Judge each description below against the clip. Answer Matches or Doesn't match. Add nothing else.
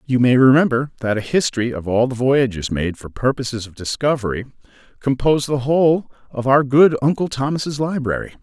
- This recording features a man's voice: Matches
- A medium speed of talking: Matches